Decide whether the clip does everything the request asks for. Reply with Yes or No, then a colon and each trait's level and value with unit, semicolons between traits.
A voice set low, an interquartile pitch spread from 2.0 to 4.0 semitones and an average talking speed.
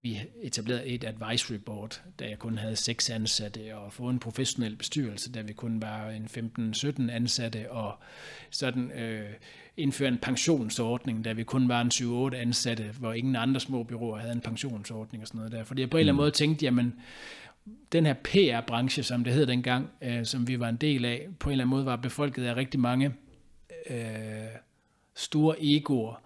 Yes: low, 120 Hz; average, 2.8 semitones; average, 190 wpm